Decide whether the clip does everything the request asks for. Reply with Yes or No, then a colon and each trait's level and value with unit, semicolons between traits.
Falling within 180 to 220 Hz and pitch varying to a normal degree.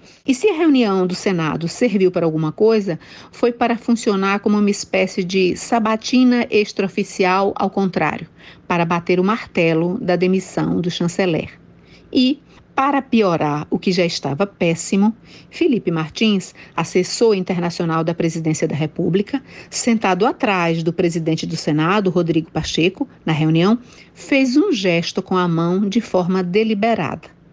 Yes: high, 190 Hz; average, 4.3 semitones